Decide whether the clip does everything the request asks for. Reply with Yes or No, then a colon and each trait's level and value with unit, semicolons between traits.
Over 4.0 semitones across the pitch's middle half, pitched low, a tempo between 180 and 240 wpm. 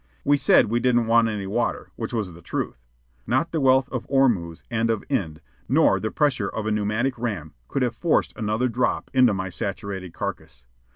Yes: average, 4.7 semitones; low, 110 Hz; average, 190 wpm